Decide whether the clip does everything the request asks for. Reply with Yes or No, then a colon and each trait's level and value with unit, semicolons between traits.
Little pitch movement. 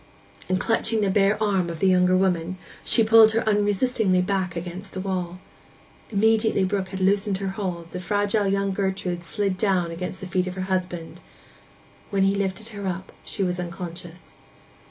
Yes: narrow, 2.0 semitones